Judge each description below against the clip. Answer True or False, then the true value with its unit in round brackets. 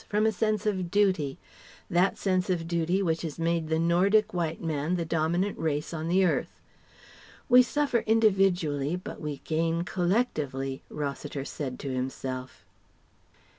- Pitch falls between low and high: True (170 Hz)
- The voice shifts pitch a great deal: False (4.2 semitones)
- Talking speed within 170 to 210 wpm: False (145 wpm)